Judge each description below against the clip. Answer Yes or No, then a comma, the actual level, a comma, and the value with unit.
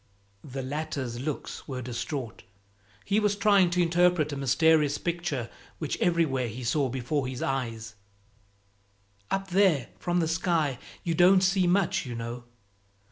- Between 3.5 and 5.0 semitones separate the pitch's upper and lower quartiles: No, wide, 5.4 semitones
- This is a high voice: No, medium, 150 Hz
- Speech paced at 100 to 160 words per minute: Yes, average, 140 wpm